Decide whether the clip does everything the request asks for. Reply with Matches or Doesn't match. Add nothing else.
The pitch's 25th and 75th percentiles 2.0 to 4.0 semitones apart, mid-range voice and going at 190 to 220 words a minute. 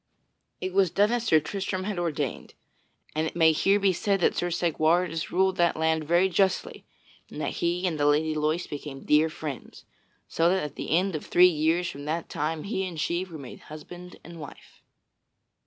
Matches